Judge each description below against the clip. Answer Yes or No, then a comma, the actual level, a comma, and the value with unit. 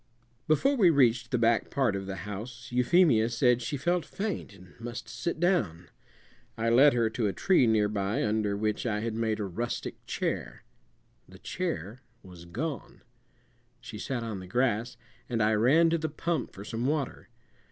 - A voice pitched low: Yes, low, 115 Hz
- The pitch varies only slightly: No, average, 5.0 semitones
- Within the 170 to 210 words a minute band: Yes, average, 175 wpm